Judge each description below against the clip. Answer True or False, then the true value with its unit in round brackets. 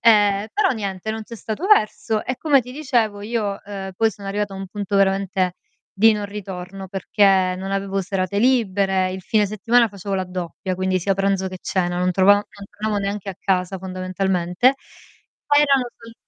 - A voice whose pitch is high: True (195 Hz)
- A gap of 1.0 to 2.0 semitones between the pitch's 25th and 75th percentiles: False (2.4 semitones)